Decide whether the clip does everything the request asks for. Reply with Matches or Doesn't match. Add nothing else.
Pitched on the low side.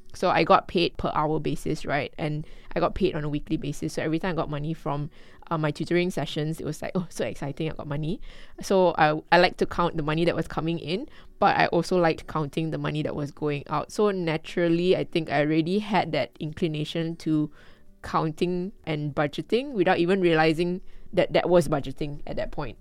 Doesn't match